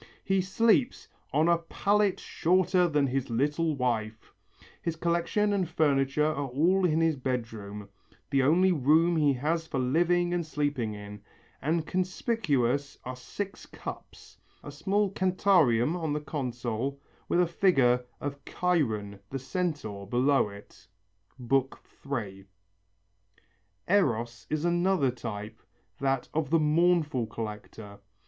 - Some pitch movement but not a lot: No, wide, 5.9 semitones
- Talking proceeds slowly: Yes, slow, 125 wpm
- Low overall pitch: No, medium, 145 Hz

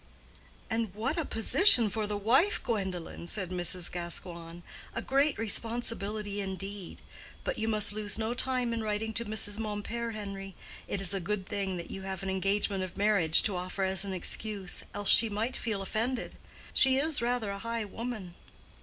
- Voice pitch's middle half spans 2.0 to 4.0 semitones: Yes, average, 3.0 semitones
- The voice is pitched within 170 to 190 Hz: No, high, 205 Hz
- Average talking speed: Yes, average, 175 wpm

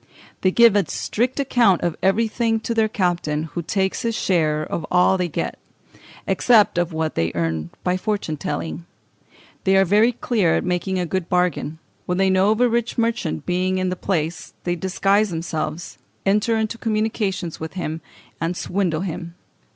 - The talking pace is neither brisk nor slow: Yes, average, 175 wpm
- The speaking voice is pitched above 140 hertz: Yes, medium, 185 Hz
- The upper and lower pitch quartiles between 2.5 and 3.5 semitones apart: No, average, 4.2 semitones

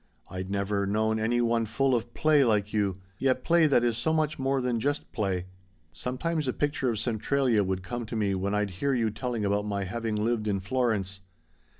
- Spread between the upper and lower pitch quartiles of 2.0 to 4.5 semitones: Yes, average, 4.1 semitones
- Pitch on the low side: Yes, low, 110 Hz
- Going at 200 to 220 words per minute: Yes, fast, 205 wpm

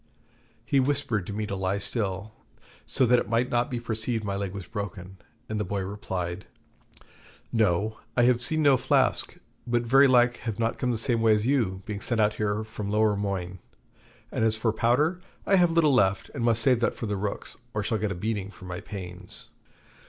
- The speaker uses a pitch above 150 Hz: No, low, 110 Hz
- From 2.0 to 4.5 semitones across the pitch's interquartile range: Yes, average, 3.4 semitones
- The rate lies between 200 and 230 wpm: Yes, fast, 205 wpm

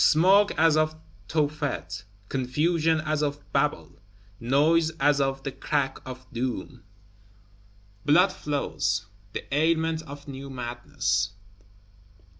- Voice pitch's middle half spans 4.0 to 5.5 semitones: No, average, 3.5 semitones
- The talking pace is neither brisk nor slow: No, slow, 105 wpm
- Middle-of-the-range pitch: Yes, medium, 145 Hz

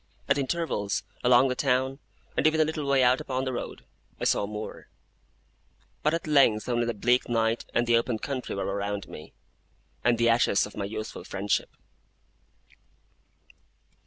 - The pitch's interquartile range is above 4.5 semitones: No, average, 3.8 semitones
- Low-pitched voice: Yes, low, 120 Hz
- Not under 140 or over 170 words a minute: Yes, average, 160 wpm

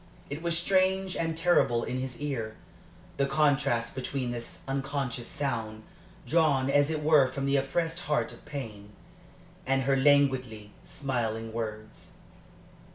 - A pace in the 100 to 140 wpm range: Yes, slow, 135 wpm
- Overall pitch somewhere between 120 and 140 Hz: Yes, low, 135 Hz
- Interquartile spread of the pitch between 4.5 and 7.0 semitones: No, average, 3.9 semitones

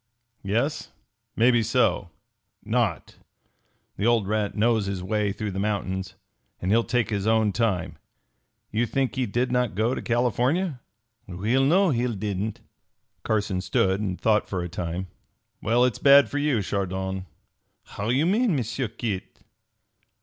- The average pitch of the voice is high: No, low, 110 Hz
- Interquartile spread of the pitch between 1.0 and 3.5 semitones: No, average, 4.1 semitones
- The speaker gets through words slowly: No, average, 150 wpm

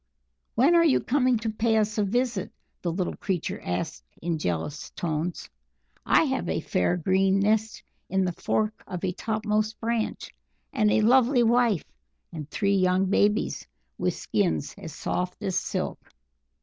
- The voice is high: Yes, high, 205 Hz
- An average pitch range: Yes, average, 3.8 semitones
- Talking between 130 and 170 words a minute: Yes, average, 160 wpm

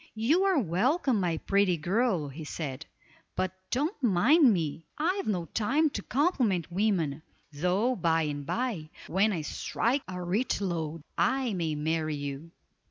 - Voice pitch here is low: No, medium, 185 Hz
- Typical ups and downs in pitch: No, wide, 7.4 semitones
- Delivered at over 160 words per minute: No, average, 150 wpm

